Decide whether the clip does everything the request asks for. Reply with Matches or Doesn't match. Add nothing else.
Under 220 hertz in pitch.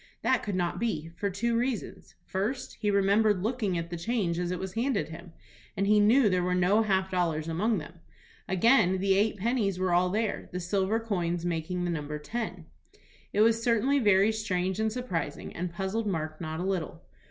Matches